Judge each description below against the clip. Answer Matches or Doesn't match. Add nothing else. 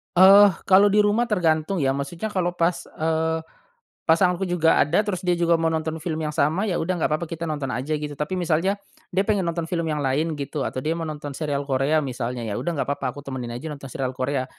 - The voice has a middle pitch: Matches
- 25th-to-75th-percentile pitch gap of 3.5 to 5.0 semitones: Matches